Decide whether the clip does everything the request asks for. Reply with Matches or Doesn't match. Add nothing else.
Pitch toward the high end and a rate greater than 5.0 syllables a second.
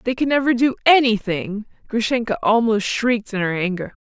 Matches